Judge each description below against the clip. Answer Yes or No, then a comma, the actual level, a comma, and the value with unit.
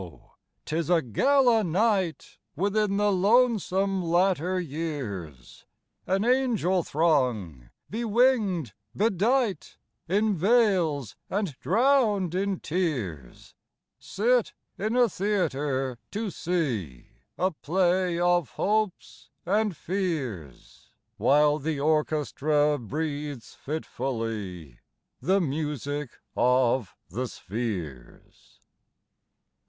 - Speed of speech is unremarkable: No, slow, 70 wpm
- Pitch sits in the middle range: Yes, medium, 170 Hz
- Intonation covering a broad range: Yes, wide, 7.1 semitones